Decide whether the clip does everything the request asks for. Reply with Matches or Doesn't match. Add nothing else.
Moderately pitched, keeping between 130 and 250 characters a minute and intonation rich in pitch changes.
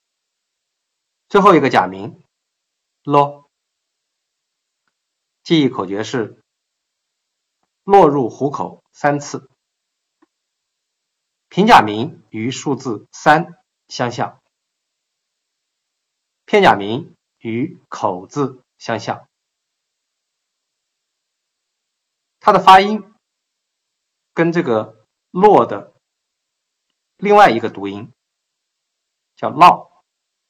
Doesn't match